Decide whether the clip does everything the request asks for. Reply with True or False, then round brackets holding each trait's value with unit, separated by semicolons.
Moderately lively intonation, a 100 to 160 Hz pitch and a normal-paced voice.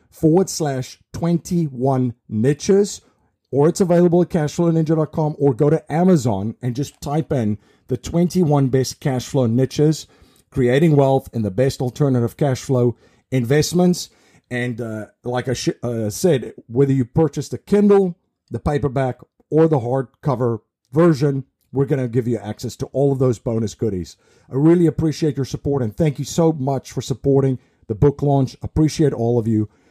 True (4.1 semitones; 135 Hz; 165 wpm)